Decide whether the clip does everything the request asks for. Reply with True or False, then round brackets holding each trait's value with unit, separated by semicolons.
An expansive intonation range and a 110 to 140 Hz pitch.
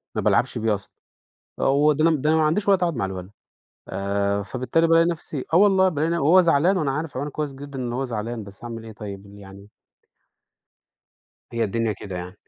True (7.1 semitones; 135 Hz)